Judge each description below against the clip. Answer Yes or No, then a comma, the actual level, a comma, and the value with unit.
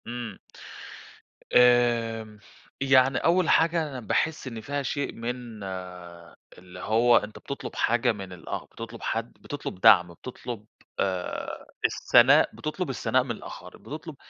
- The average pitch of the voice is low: Yes, low, 120 Hz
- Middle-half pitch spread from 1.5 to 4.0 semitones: Yes, average, 3.5 semitones